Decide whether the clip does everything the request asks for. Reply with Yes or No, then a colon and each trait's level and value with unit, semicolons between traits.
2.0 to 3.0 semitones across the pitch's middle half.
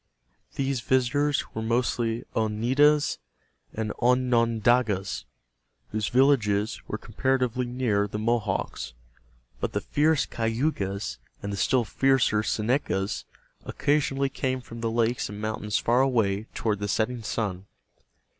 No: average, 3.5 semitones